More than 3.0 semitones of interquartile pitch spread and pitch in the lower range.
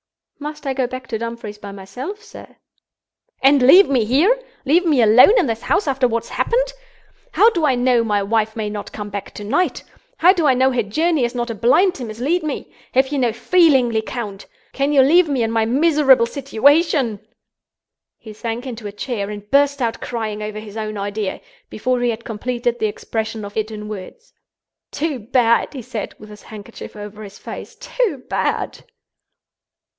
No: average, 4.8 semitones; high, 240 Hz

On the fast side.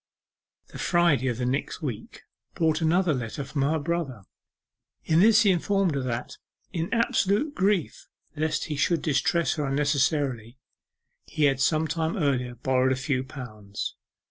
No: average, 150 wpm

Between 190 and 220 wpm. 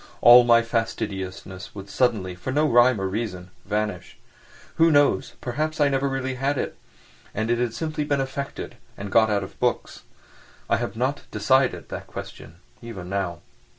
No: average, 170 wpm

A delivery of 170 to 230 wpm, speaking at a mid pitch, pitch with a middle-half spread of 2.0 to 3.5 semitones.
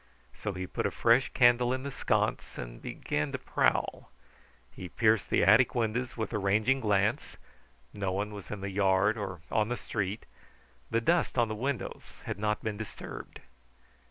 No: average, 175 wpm; low, 105 Hz; average, 3.2 semitones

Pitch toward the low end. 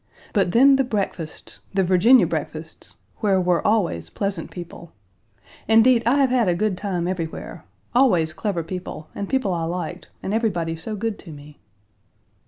No: medium, 185 Hz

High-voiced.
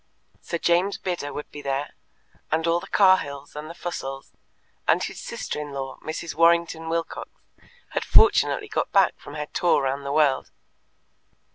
No: medium, 160 Hz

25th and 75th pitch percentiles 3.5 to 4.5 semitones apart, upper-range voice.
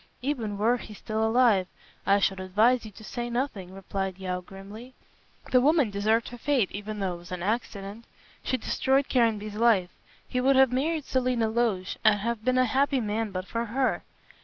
Yes: average, 4.0 semitones; high, 220 Hz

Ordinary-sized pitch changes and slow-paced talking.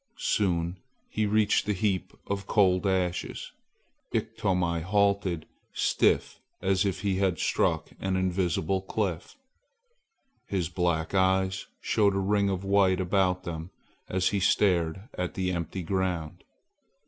No: narrow, 1.8 semitones; slow, 125 wpm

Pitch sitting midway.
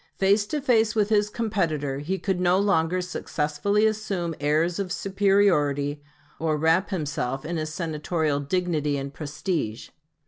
Yes: medium, 170 Hz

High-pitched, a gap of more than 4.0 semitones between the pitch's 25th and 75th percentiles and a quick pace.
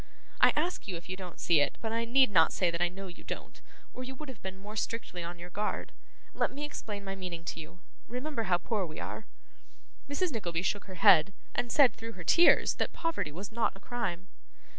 Yes: high, 195 Hz; average, 5.2 semitones; fast, 225 wpm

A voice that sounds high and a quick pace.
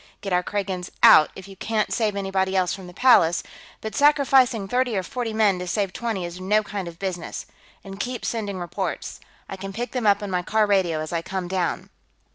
Yes: high, 195 Hz; fast, 215 wpm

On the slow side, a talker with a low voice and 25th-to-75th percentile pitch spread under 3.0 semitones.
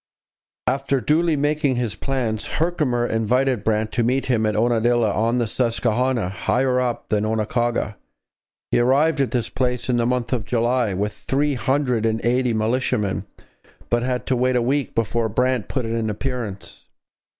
No: average, 165 wpm; low, 120 Hz; narrow, 2.6 semitones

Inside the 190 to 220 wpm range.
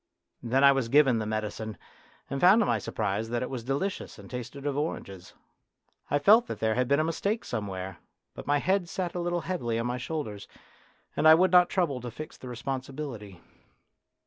Yes: average, 200 wpm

